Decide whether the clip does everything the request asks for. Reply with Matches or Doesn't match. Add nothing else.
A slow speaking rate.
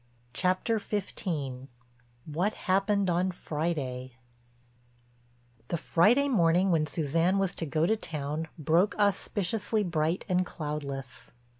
Matches